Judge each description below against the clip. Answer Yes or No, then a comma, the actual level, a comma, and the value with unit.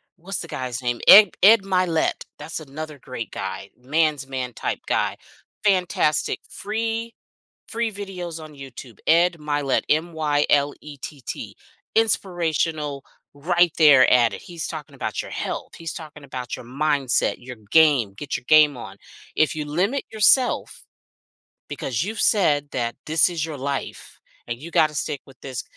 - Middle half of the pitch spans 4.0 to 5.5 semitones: Yes, average, 4.3 semitones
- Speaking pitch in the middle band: Yes, medium, 150 Hz